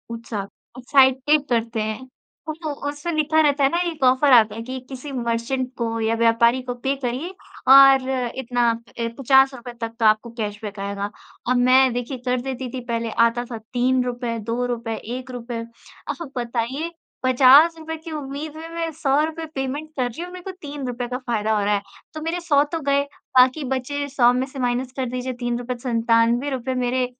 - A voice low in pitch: No, very high, 255 Hz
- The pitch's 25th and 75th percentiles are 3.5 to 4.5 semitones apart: No, average, 3.1 semitones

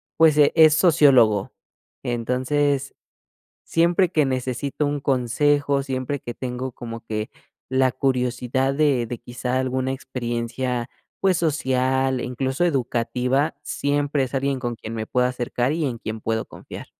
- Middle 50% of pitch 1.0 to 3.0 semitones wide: Yes, narrow, 2.6 semitones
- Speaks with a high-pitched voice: No, low, 130 Hz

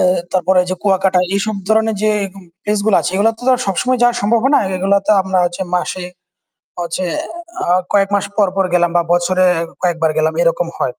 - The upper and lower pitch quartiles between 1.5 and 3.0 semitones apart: Yes, average, 2.7 semitones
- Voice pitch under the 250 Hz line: Yes, high, 190 Hz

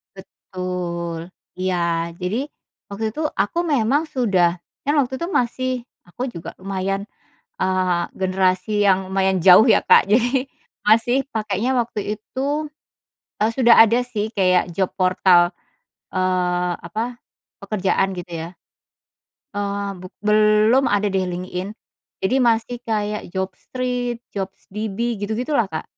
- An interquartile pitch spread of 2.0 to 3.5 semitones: No, average, 4.0 semitones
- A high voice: Yes, high, 200 Hz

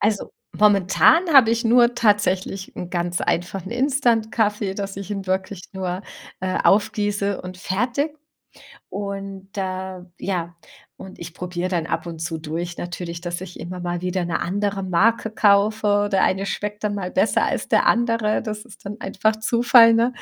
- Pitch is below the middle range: No, high, 195 Hz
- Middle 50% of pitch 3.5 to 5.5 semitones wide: No, average, 2.9 semitones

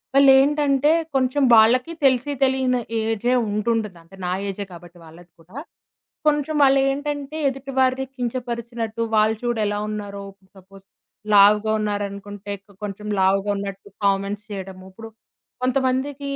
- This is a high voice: Yes, high, 225 Hz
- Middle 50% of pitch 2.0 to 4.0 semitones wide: No, average, 4.9 semitones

